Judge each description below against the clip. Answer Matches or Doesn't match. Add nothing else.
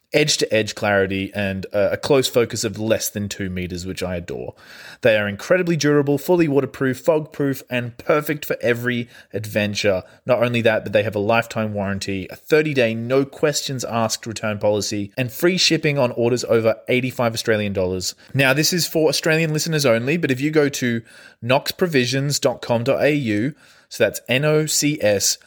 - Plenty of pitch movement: Matches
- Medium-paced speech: Matches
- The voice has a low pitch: Matches